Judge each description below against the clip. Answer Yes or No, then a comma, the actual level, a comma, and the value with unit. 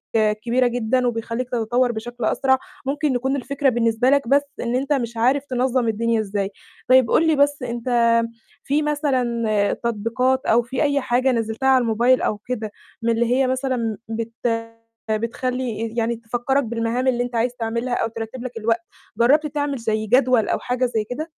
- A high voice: Yes, high, 240 Hz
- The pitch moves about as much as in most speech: No, narrow, 2.3 semitones